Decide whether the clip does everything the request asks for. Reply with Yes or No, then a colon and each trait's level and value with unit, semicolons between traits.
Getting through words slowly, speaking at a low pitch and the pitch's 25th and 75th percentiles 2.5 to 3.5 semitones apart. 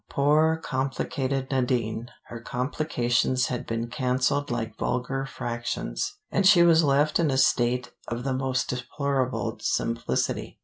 Yes: slow, 130 wpm; low, 130 Hz; average, 2.8 semitones